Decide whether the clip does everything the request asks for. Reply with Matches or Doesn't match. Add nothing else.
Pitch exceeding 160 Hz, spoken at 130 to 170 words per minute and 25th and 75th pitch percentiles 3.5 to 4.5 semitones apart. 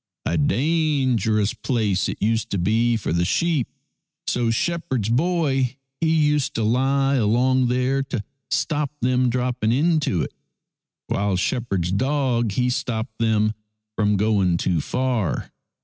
Doesn't match